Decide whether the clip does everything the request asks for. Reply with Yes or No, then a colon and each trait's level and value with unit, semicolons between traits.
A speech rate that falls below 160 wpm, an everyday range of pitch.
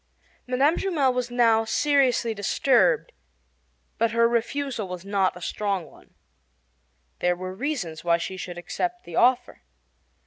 No: slow, 135 wpm; wide, 6.3 semitones